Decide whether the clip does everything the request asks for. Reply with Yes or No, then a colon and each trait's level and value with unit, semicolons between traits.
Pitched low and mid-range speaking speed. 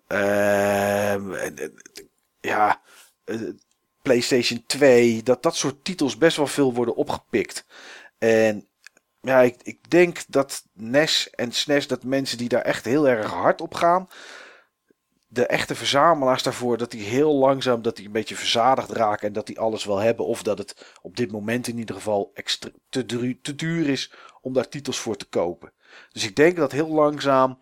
Yes: low, 125 Hz; average, 170 wpm